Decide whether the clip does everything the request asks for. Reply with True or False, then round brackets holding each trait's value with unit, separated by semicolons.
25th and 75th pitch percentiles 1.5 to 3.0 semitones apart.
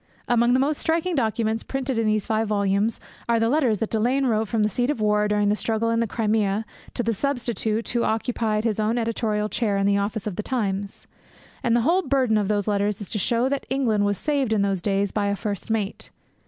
True (2.5 semitones)